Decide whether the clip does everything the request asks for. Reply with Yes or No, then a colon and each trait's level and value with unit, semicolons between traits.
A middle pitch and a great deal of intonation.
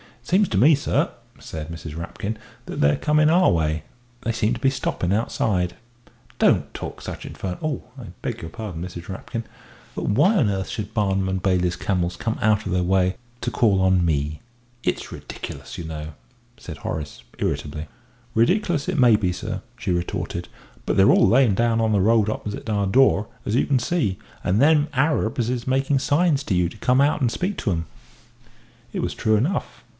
No: low, 105 Hz; wide, 6.3 semitones